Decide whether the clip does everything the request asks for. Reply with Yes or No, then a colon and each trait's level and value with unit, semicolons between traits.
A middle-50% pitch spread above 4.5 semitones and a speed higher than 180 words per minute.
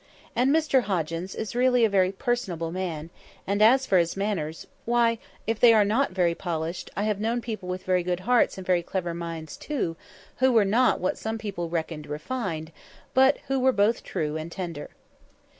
Yes: wide, 5.5 semitones; average, 190 wpm